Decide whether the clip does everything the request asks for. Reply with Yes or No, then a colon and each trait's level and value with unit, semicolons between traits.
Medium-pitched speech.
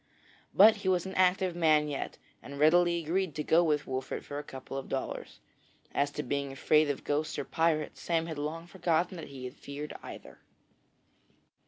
Yes: medium, 155 Hz